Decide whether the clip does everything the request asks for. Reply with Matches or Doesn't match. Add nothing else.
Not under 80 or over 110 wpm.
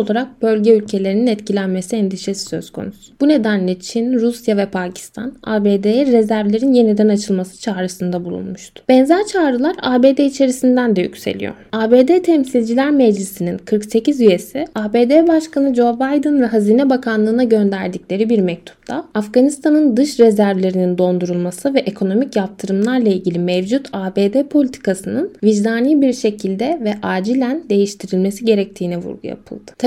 Doesn't match